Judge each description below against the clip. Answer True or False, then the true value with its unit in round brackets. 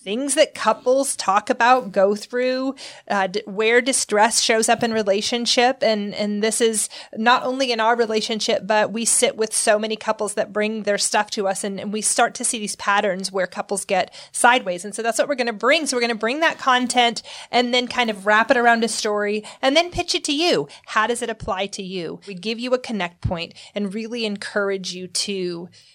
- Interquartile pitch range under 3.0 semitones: False (3.3 semitones)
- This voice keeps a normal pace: False (220 wpm)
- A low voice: False (220 Hz)